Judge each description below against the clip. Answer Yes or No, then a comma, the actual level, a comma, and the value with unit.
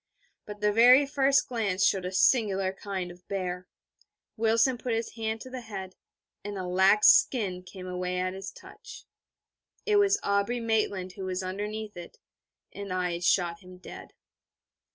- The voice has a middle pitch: No, high, 200 Hz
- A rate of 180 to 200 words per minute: No, average, 170 wpm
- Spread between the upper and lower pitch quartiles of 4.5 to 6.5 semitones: No, average, 3.6 semitones